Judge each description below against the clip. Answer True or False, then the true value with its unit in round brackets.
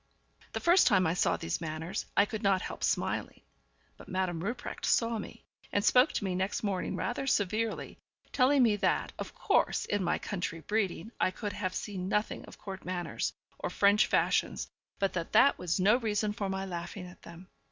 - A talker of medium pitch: False (195 Hz)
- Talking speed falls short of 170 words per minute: False (190 wpm)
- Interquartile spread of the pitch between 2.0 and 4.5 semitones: True (2.9 semitones)